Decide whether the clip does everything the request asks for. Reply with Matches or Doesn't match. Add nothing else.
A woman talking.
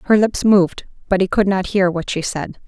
Matches